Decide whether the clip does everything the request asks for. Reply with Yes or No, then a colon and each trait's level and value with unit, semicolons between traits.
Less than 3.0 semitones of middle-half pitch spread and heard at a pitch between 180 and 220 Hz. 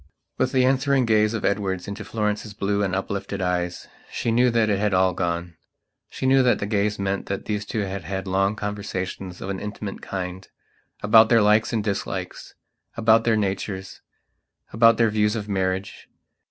No: narrow, 2.5 semitones; low, 105 Hz